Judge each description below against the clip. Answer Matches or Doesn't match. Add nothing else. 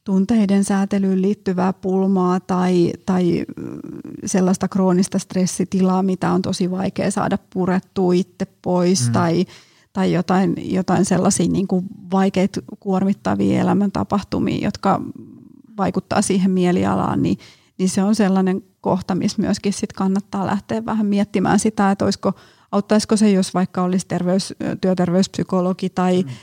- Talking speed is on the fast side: Doesn't match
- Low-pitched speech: Doesn't match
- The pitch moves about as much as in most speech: Doesn't match